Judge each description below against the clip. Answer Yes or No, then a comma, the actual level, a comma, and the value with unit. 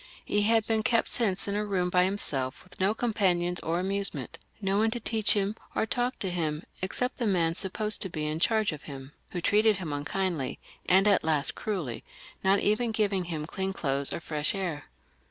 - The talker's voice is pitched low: No, high, 190 Hz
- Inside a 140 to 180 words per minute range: No, fast, 205 wpm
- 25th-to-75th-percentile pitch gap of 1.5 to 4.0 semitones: No, average, 4.5 semitones